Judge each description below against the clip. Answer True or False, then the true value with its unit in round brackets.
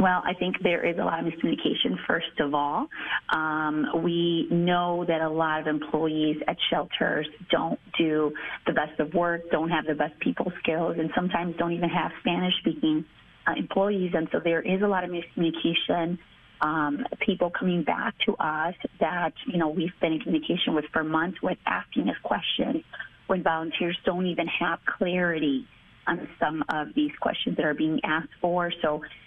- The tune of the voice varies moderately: False (2.3 semitones)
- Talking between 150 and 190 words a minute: True (180 wpm)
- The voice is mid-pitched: True (170 Hz)